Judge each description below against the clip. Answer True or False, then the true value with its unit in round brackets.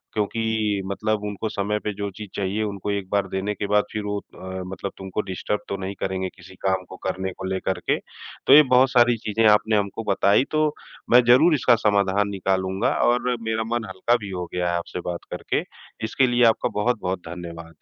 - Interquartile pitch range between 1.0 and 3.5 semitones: True (2.8 semitones)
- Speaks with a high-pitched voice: False (100 Hz)